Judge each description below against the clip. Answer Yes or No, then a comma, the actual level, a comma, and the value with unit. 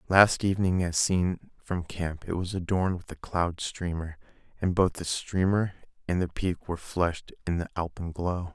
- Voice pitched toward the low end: Yes, very low, 90 Hz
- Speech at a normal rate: Yes, average, 175 wpm